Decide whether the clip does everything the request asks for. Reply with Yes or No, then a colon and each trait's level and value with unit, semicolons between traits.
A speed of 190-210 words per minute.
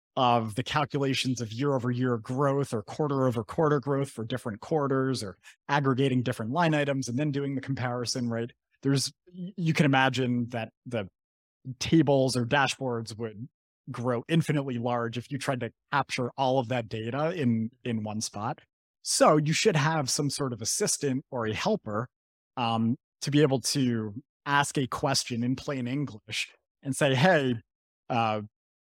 No: average, 165 wpm